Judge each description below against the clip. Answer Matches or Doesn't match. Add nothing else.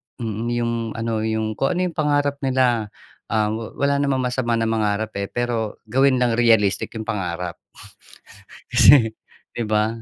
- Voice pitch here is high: Doesn't match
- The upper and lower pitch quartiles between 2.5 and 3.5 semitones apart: Matches